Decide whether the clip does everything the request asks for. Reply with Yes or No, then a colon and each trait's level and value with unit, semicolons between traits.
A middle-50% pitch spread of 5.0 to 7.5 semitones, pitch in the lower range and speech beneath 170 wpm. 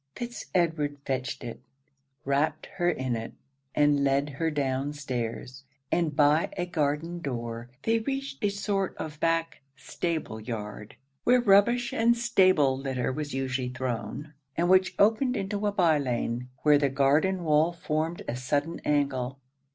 No: average, 5.3 semitones; medium, 150 Hz; average, 150 wpm